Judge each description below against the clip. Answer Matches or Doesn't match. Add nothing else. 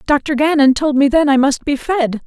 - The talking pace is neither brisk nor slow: Doesn't match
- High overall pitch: Matches